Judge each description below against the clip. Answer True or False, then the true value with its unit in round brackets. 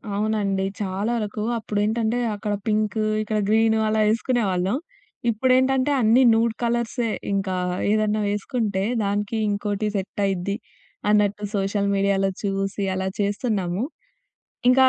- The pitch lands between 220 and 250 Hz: False (210 Hz)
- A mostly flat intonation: True (2.1 semitones)